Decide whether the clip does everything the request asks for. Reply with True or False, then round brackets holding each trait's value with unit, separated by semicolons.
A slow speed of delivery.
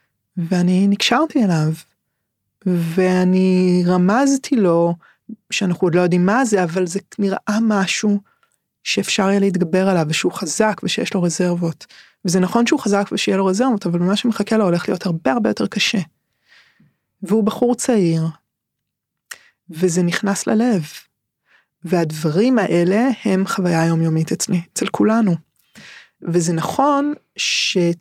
False (125 wpm)